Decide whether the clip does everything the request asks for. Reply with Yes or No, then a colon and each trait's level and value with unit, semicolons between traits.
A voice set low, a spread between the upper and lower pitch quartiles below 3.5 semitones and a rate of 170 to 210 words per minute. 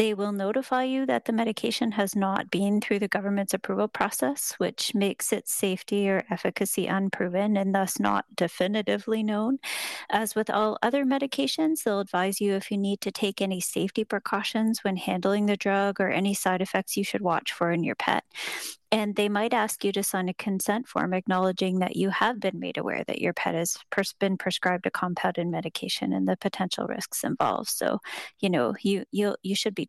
No: high, 200 Hz; narrow, 2.4 semitones; average, 195 wpm